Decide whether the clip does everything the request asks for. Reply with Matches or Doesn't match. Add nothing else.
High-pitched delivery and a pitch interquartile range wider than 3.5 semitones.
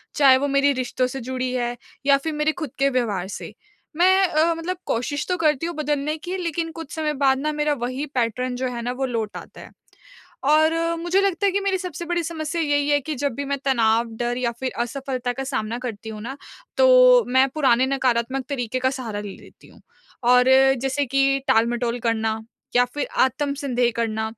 Matches